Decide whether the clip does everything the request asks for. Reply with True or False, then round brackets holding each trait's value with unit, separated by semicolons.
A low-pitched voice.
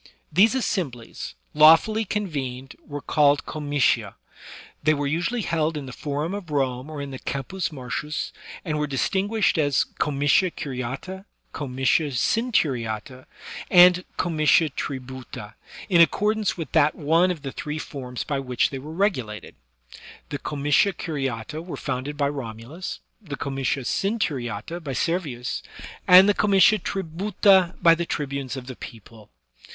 False (150 Hz)